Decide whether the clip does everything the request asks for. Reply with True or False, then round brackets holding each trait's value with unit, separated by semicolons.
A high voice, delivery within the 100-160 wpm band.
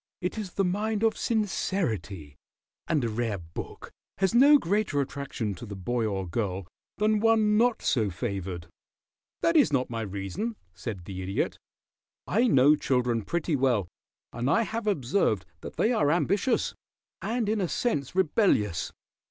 False (140 Hz; 155 wpm)